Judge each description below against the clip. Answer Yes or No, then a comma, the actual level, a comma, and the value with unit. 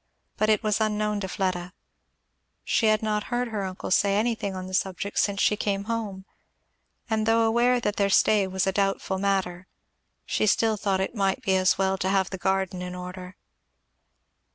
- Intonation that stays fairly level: Yes, narrow, 2.2 semitones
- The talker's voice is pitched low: No, high, 200 Hz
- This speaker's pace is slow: No, average, 185 wpm